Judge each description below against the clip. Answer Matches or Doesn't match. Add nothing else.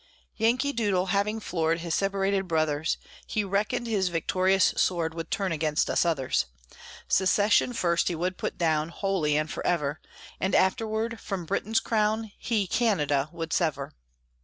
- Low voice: Doesn't match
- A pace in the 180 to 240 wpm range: Doesn't match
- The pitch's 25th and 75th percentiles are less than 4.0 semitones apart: Doesn't match